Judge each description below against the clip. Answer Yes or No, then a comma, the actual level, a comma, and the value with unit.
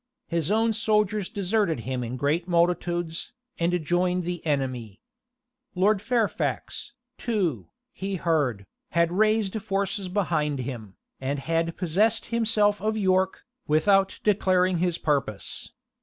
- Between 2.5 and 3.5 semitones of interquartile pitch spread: No, average, 4.9 semitones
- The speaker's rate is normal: No, slow, 120 wpm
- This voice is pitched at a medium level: Yes, medium, 180 Hz